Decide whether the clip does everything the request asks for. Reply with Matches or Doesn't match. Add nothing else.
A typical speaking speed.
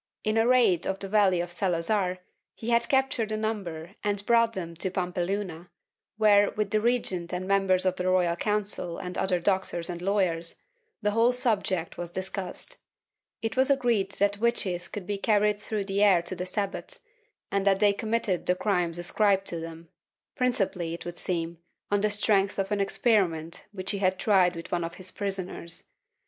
Matches